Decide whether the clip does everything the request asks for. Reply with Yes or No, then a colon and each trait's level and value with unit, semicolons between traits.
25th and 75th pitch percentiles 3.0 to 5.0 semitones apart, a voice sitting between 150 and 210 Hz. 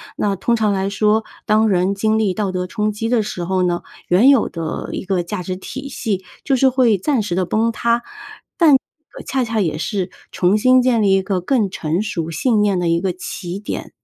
Yes: average, 3.9 semitones; high, 205 Hz